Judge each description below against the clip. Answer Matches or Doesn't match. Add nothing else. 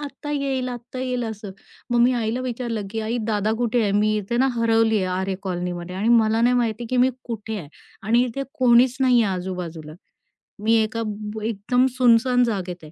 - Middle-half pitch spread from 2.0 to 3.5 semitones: Matches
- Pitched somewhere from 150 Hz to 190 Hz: Doesn't match